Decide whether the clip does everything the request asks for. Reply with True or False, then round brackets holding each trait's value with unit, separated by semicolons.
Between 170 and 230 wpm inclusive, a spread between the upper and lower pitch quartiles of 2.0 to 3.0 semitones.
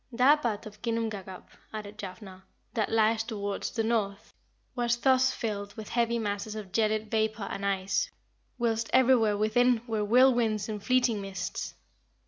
False (145 wpm; 2.5 semitones)